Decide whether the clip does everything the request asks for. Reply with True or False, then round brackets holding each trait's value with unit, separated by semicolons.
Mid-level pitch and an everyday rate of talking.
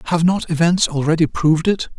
True (165 Hz; 180 wpm)